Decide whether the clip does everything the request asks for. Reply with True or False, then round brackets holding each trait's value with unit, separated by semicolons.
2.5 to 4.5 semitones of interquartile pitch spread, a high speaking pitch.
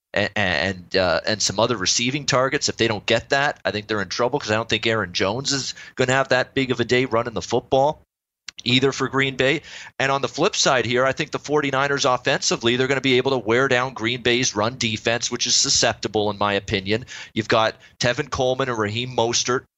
False (3.1 semitones; 125 Hz)